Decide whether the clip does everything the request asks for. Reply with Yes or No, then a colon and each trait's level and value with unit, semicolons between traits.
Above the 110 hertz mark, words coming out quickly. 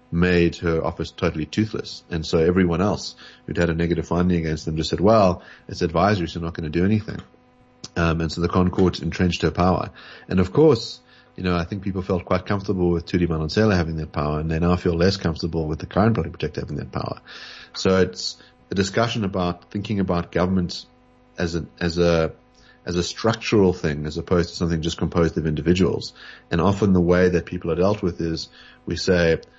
No: very low, 85 Hz; fast, 210 wpm